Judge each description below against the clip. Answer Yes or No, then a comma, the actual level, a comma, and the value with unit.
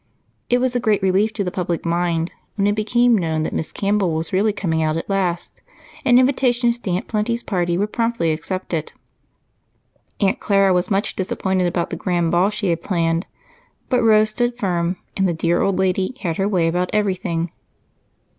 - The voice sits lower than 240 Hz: Yes, high, 190 Hz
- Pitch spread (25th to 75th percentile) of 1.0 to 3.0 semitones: No, average, 3.7 semitones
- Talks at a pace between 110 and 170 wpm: No, average, 185 wpm